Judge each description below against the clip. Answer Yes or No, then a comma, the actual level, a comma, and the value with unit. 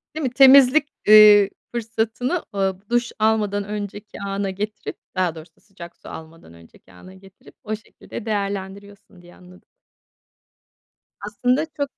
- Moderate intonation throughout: Yes, average, 3.1 semitones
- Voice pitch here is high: Yes, high, 205 Hz